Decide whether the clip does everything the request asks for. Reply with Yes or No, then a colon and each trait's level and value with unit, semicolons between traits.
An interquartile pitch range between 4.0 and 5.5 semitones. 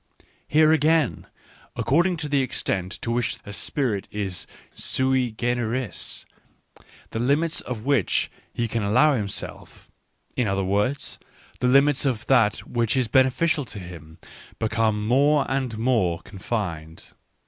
Yes: average, 4.8 semitones